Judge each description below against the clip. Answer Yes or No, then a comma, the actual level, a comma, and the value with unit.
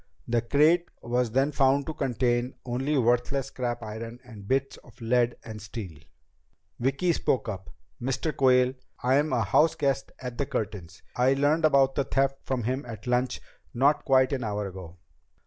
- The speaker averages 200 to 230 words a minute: No, average, 165 wpm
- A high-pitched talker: No, low, 125 Hz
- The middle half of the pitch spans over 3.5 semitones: No, average, 2.9 semitones